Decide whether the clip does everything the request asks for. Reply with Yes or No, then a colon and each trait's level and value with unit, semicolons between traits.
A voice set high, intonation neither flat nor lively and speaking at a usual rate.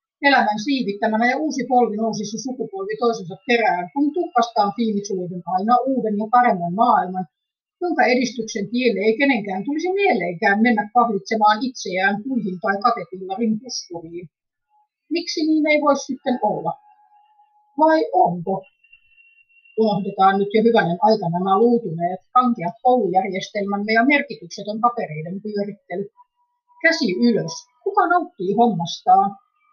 No: high, 230 Hz; wide, 6.1 semitones; average, 115 wpm